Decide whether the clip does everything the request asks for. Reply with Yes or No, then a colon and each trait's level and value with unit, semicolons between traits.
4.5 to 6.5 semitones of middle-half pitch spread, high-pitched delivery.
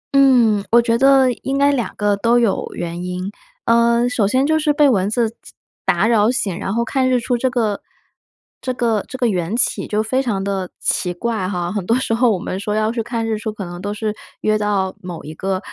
No: average, 3.7 semitones; high, 220 Hz